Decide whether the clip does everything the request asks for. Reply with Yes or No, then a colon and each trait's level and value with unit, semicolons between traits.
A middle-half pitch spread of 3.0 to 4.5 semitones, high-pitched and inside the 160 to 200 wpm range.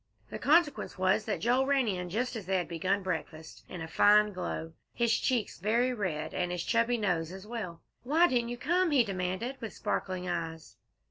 No: average, 5.3 semitones; high, 205 Hz; average, 195 wpm